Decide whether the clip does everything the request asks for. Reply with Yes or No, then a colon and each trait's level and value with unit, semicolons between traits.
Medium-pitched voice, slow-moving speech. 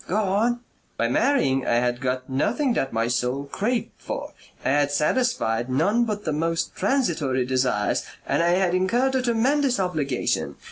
No: medium, 165 Hz; average, 160 wpm